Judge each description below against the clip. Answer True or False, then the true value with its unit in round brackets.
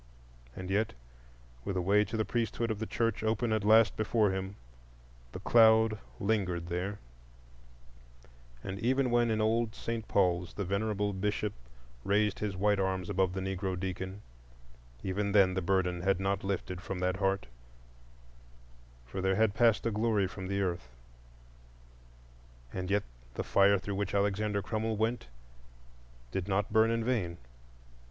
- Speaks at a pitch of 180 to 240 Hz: False (100 Hz)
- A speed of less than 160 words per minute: True (150 wpm)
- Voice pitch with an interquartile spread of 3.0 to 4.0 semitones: False (2.6 semitones)